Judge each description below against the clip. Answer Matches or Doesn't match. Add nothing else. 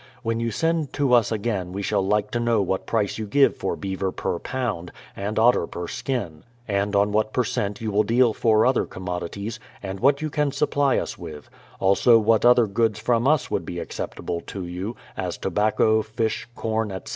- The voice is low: Matches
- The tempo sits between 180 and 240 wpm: Matches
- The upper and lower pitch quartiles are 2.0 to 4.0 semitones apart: Matches